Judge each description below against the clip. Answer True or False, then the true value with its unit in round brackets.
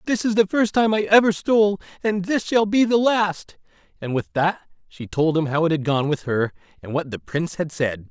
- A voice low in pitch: False (180 Hz)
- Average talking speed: False (235 wpm)